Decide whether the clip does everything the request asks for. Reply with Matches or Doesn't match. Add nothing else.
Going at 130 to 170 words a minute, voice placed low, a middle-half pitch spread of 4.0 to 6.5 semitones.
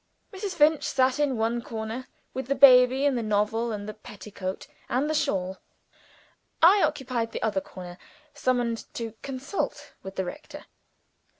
Doesn't match